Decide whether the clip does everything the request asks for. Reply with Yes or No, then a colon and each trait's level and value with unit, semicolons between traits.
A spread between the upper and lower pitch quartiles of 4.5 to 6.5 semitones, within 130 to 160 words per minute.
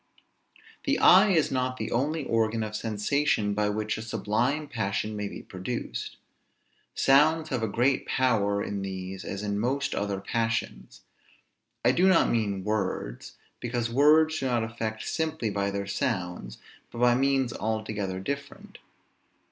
Yes: average, 4.9 semitones; average, 150 wpm